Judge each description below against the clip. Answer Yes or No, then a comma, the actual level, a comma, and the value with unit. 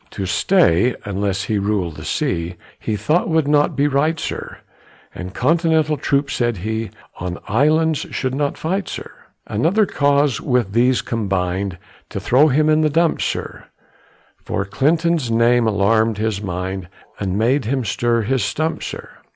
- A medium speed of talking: Yes, average, 155 wpm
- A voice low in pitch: Yes, low, 120 Hz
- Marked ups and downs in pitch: Yes, wide, 6.9 semitones